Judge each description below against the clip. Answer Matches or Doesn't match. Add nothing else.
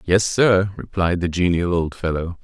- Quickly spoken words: Doesn't match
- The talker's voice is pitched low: Matches